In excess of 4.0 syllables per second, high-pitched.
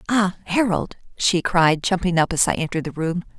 No: 5.5 syllables/s; medium, 180 Hz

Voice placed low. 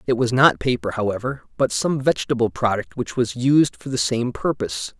Yes: low, 125 Hz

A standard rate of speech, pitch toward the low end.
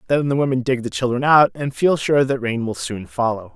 No: fast, 255 wpm; low, 125 Hz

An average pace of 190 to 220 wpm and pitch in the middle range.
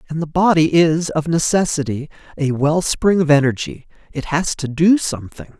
No: average, 160 wpm; medium, 155 Hz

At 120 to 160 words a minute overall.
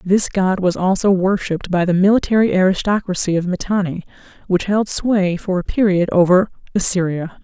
Yes: average, 155 wpm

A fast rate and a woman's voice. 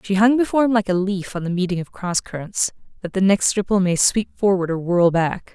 Yes: fast, 250 wpm; female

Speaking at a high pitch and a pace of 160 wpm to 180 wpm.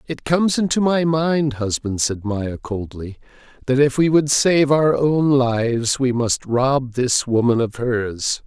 No: low, 130 Hz; average, 170 wpm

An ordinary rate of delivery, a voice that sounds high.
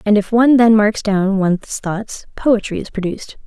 Yes: average, 190 wpm; high, 210 Hz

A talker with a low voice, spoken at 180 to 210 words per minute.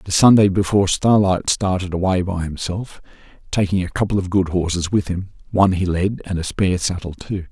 Yes: very low, 95 Hz; average, 185 wpm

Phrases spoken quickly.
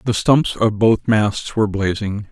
No: average, 180 wpm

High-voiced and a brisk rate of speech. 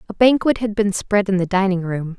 Yes: high, 200 Hz; fast, 245 wpm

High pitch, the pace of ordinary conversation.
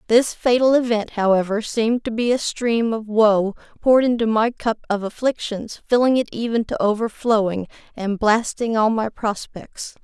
Yes: high, 225 Hz; average, 160 wpm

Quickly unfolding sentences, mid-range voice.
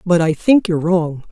Yes: fast, 230 wpm; medium, 175 Hz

